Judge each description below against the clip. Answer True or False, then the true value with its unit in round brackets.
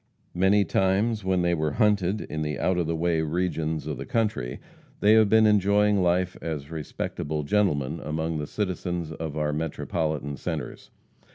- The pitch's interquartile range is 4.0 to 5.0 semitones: True (4.4 semitones)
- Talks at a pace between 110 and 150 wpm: False (165 wpm)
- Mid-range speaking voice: False (85 Hz)